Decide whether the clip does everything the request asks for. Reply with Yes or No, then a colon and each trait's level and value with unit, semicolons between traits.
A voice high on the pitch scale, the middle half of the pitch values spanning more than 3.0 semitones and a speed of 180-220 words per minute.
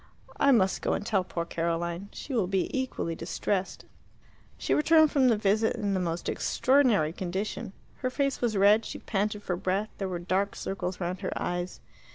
Yes: high, 195 Hz; average, 4.2 semitones; average, 185 wpm